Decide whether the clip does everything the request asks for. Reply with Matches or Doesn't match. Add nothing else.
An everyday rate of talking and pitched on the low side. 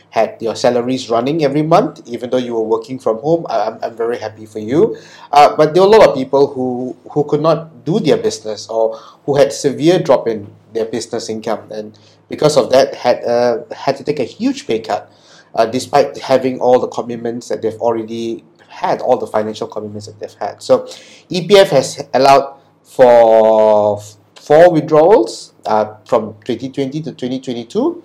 Matches